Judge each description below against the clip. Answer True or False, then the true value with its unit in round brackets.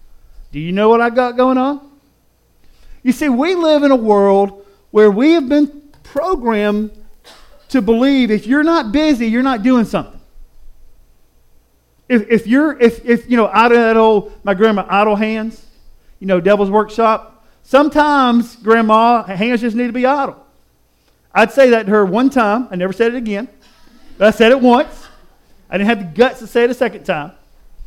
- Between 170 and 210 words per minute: True (185 wpm)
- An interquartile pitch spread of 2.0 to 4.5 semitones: True (4.0 semitones)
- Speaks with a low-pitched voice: False (225 Hz)